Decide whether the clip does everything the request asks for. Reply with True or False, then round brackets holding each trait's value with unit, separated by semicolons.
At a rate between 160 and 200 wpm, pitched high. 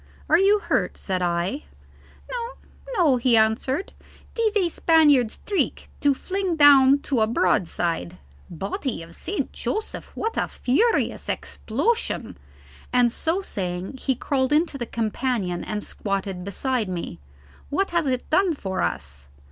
False (140 wpm; 260 Hz)